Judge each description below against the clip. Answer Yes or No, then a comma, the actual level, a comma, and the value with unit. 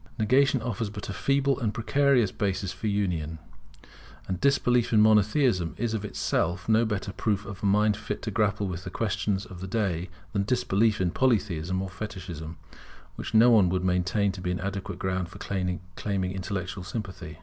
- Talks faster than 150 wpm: Yes, average, 180 wpm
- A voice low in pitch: Yes, low, 100 Hz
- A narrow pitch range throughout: No, average, 3.1 semitones